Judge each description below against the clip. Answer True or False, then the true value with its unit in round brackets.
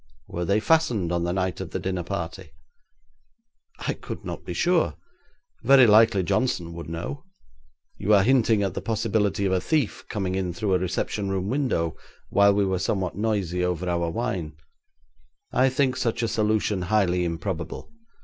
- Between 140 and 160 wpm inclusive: False (170 wpm)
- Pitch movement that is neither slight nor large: True (3.8 semitones)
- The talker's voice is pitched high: False (95 Hz)